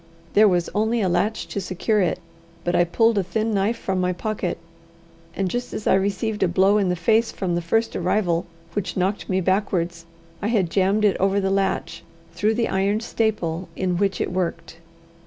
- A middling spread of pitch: Yes, average, 3.0 semitones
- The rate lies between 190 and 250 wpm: Yes, average, 195 wpm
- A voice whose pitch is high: Yes, high, 195 Hz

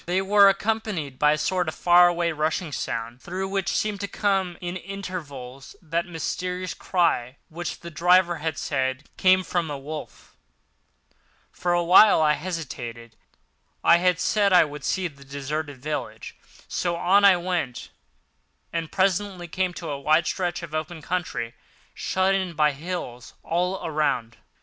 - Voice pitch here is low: No, medium, 170 Hz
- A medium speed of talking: Yes, average, 155 wpm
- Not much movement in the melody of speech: No, average, 3.7 semitones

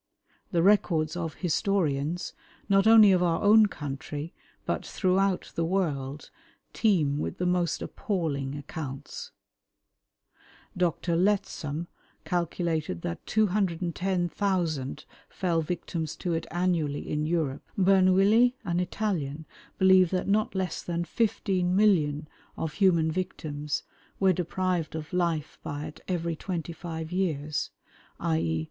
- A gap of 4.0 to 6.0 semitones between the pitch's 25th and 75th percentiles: No, average, 3.5 semitones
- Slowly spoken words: Yes, slow, 115 wpm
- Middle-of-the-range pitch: Yes, medium, 170 Hz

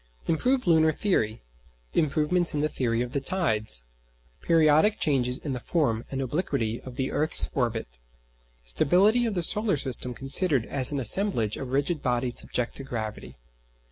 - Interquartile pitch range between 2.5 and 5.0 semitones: No, wide, 5.5 semitones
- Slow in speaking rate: No, average, 155 wpm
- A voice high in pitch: No, medium, 140 Hz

